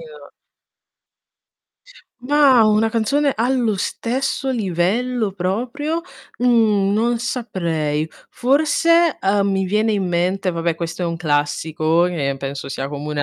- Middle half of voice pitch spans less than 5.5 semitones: No, wide, 6.7 semitones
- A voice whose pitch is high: Yes, high, 205 Hz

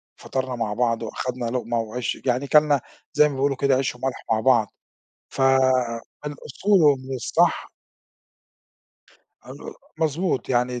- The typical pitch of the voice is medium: No, low, 130 Hz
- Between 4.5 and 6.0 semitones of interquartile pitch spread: No, narrow, 2.4 semitones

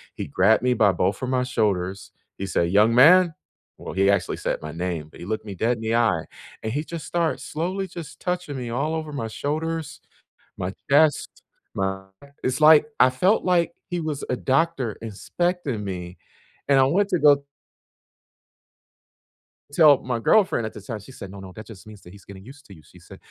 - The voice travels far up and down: Yes, wide, 7.7 semitones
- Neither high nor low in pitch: No, low, 125 Hz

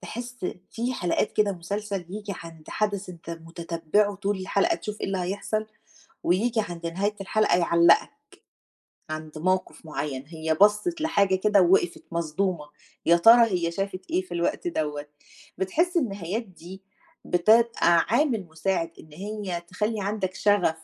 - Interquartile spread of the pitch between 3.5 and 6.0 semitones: Yes, average, 3.8 semitones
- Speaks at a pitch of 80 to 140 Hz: No, high, 190 Hz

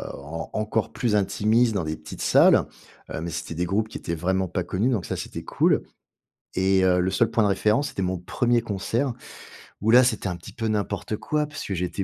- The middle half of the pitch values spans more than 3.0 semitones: Yes, average, 3.8 semitones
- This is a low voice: Yes, low, 100 Hz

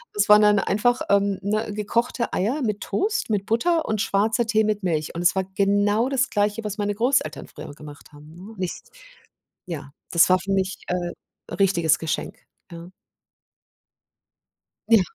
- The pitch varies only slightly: No, average, 3.1 semitones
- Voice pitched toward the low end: No, high, 205 Hz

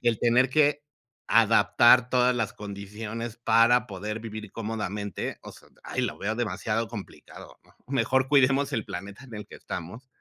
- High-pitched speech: No, low, 115 Hz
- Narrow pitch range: No, average, 3.0 semitones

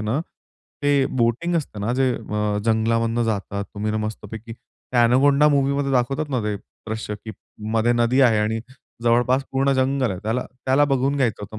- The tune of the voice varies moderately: Yes, average, 3.6 semitones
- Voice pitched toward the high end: No, low, 120 Hz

